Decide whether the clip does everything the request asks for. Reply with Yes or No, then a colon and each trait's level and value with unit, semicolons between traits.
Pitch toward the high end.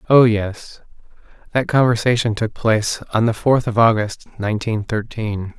No: low, 110 Hz